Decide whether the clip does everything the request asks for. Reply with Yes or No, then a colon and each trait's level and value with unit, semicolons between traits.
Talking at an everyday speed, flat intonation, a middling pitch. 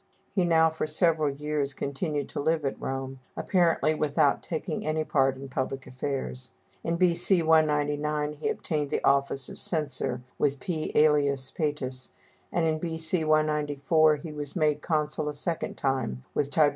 Yes: average, 160 wpm; narrow, 2.3 semitones; medium, 150 Hz